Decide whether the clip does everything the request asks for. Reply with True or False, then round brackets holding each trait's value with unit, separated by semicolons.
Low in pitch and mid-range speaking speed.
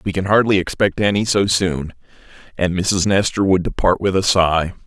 True (95 Hz; 185 wpm)